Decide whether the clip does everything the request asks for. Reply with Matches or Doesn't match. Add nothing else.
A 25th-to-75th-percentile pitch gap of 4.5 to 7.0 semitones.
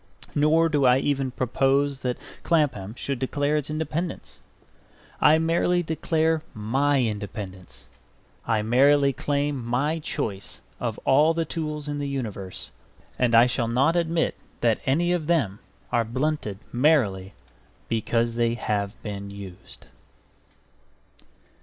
Matches